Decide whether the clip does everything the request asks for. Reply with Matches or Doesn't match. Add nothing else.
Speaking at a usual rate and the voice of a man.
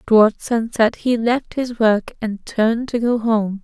Doesn't match